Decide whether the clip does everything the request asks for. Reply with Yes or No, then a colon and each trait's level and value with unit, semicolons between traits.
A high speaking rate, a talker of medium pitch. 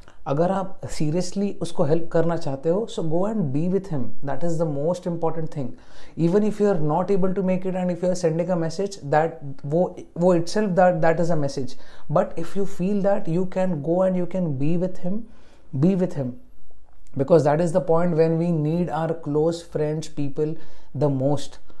Yes: fast, 210 wpm; medium, 170 Hz